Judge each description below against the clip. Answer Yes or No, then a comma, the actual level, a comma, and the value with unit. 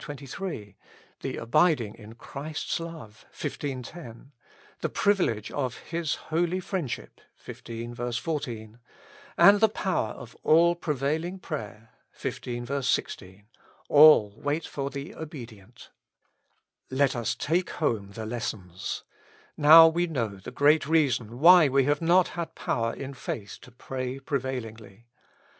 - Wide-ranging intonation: Yes, wide, 5.7 semitones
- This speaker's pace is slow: Yes, slow, 125 wpm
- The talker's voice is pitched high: No, low, 135 Hz